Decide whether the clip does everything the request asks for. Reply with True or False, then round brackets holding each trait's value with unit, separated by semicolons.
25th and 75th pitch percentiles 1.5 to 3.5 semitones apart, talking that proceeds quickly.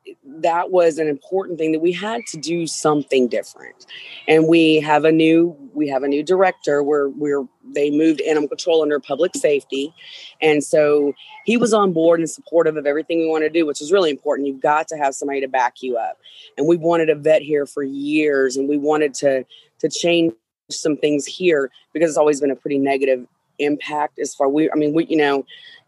True (2.8 semitones; 210 wpm)